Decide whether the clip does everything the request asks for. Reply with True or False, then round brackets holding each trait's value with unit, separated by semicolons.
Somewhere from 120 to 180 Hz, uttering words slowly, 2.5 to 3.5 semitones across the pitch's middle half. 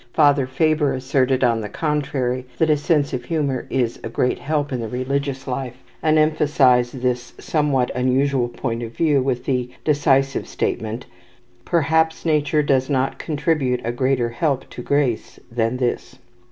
False (135 Hz; 155 wpm; 2.9 semitones)